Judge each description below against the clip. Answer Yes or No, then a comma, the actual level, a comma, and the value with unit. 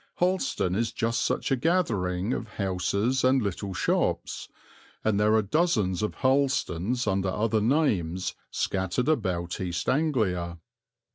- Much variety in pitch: Yes, wide, 5.9 semitones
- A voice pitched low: Yes, low, 105 Hz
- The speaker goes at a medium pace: No, slow, 130 wpm